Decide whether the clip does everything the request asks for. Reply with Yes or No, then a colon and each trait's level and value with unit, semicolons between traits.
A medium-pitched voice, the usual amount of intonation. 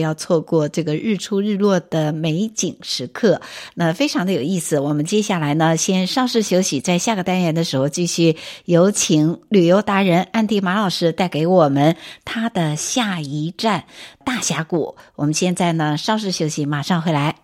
Yes: medium, 175 Hz; average, 3.9 semitones